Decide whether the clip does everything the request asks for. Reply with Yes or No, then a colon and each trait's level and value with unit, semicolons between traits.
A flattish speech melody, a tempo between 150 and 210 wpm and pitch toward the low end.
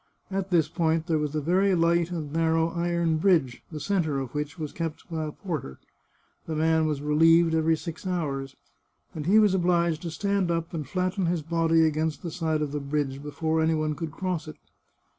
No: narrow, 2.1 semitones; average, 200 wpm; medium, 160 Hz